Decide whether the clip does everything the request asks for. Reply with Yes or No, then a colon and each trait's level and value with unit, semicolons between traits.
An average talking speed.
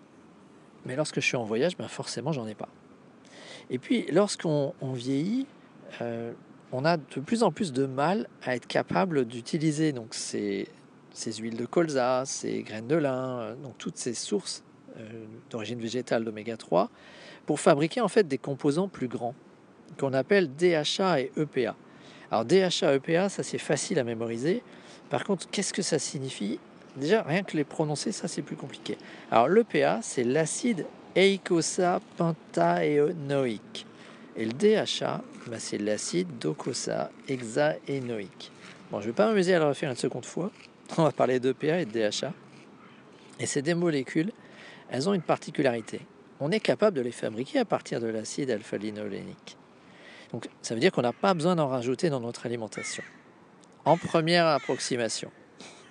Yes: average, 165 wpm